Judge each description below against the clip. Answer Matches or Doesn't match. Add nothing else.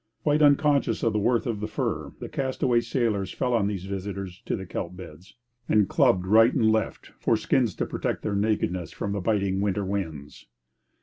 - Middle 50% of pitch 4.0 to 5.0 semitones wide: Doesn't match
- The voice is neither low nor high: Doesn't match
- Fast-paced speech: Doesn't match